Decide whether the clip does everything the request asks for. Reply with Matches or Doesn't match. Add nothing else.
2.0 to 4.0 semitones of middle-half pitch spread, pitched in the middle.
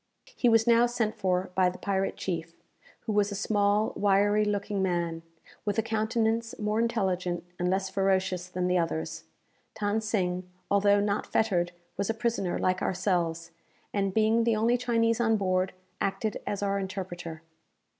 Doesn't match